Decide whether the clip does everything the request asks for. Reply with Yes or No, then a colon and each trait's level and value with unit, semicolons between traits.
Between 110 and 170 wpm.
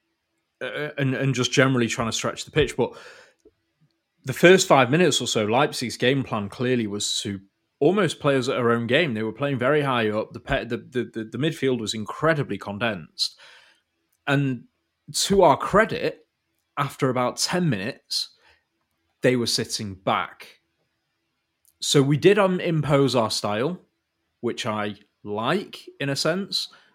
Yes: average, 155 wpm